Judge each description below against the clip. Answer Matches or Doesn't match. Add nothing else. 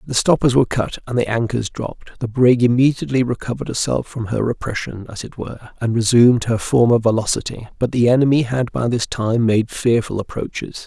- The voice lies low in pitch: Matches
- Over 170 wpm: Matches